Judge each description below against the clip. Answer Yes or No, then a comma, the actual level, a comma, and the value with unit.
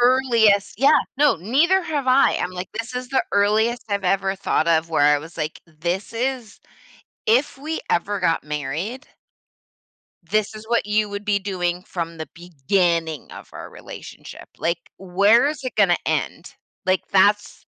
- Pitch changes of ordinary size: No, wide, 5.8 semitones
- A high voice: Yes, high, 200 Hz